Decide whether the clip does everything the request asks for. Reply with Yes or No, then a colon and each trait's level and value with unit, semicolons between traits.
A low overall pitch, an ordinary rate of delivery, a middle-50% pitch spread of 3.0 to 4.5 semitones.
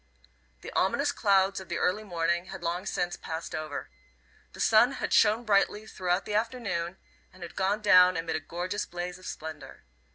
No: medium, 185 Hz; average, 175 wpm; average, 3.3 semitones